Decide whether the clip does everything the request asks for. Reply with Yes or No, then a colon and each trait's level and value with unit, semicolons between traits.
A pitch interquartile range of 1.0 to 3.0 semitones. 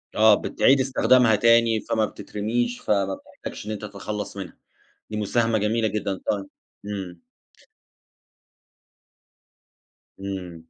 Yes: narrow, 2.6 semitones